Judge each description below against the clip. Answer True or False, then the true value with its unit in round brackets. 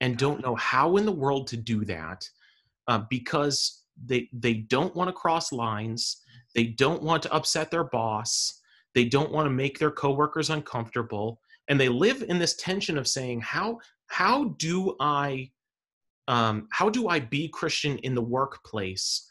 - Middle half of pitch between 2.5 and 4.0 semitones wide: False (4.7 semitones)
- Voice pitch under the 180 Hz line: True (135 Hz)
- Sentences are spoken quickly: False (170 wpm)